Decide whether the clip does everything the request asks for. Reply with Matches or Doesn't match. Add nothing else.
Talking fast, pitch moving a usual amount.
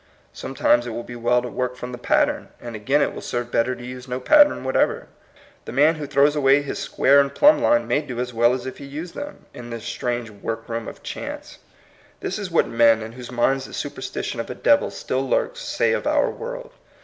Matches